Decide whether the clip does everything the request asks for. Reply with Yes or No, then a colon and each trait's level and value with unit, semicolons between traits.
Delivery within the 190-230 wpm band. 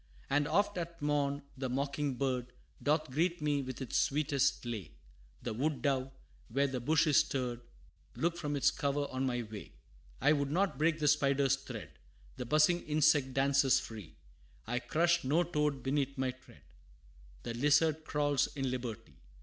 No: average, 165 wpm